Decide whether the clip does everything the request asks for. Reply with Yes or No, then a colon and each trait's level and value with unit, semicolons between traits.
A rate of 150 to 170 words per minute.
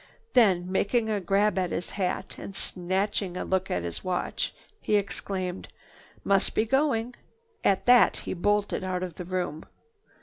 Yes: average, 160 wpm